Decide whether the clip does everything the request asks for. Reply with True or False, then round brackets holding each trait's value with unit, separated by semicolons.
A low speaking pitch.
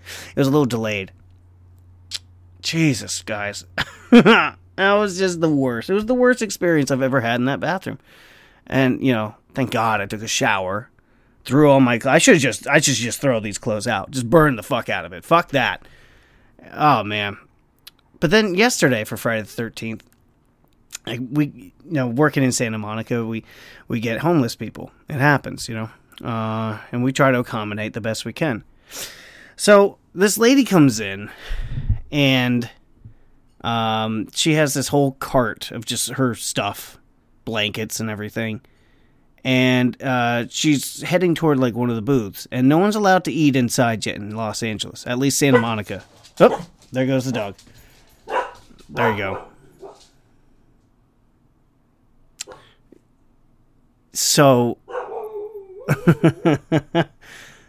True (125 Hz)